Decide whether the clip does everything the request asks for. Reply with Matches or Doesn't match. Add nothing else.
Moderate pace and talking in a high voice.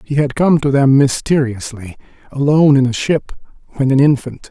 Doesn't match